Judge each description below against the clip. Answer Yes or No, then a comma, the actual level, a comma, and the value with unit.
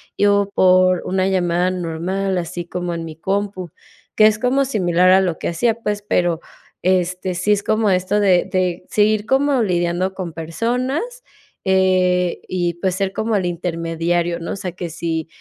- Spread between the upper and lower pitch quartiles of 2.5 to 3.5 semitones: Yes, average, 2.8 semitones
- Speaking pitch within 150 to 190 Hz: Yes, medium, 185 Hz